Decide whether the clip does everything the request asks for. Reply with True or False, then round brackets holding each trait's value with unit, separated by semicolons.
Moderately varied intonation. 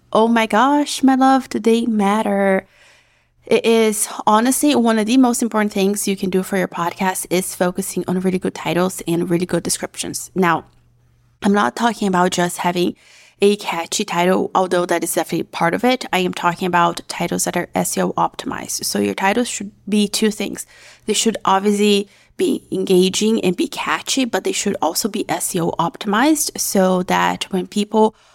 True (3.8 semitones)